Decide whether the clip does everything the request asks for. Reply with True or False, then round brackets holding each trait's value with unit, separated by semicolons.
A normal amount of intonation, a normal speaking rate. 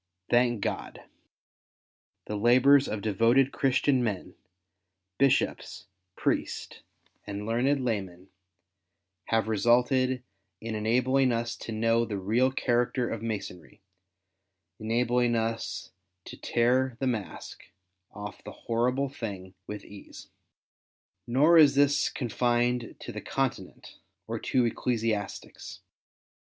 False (3.4 semitones; 115 wpm)